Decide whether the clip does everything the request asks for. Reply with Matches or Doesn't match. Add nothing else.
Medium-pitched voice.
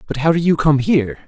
Matches